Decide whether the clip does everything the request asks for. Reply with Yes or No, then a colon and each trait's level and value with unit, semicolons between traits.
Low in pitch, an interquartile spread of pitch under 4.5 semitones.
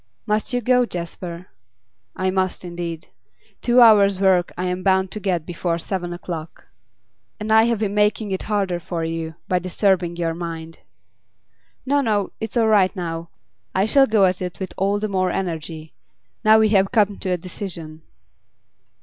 No: medium, 185 Hz; average, 3.3 semitones